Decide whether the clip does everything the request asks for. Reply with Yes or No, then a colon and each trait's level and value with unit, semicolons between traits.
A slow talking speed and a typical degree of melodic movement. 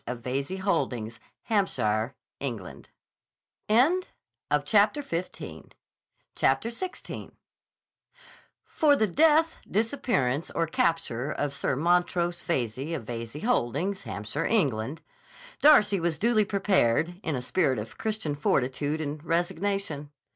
No: slow, 100 wpm; wide, 7.7 semitones